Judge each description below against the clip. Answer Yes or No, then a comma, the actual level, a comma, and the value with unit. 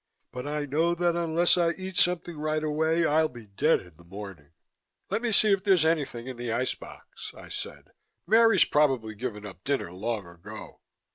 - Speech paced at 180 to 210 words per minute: Yes, average, 185 wpm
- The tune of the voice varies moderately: No, wide, 7.7 semitones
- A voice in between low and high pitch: Yes, medium, 150 Hz